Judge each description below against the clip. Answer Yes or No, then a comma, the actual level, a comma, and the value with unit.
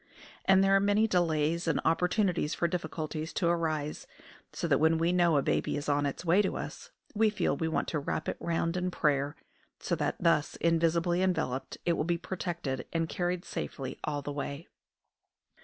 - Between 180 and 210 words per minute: Yes, average, 190 wpm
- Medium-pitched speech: Yes, medium, 165 Hz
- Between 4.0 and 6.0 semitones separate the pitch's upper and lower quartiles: No, average, 2.9 semitones